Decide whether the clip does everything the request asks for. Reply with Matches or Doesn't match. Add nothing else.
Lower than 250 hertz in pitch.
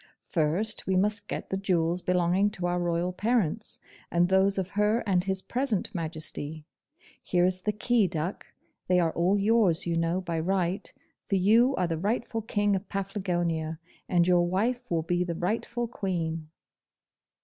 Matches